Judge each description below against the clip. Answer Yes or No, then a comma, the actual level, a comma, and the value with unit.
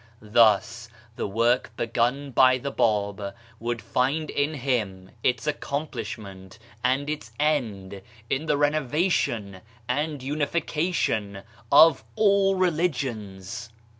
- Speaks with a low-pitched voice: Yes, low, 125 Hz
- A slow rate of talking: Yes, slow, 105 wpm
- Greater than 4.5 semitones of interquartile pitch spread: Yes, wide, 5.6 semitones